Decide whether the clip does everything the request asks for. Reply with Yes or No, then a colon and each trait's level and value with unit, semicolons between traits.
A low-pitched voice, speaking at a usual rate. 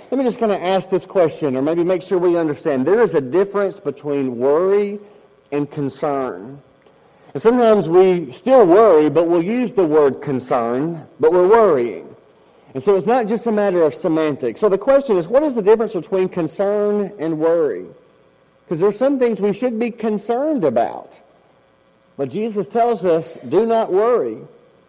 No: high, 190 Hz; average, 175 wpm